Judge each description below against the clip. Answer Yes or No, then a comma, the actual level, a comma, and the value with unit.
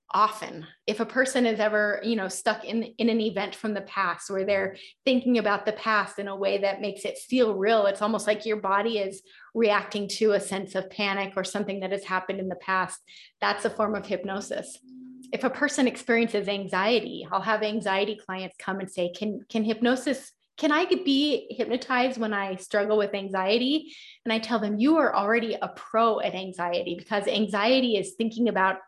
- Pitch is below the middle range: No, high, 210 Hz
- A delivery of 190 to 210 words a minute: Yes, average, 195 wpm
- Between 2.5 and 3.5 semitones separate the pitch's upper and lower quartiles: Yes, average, 2.9 semitones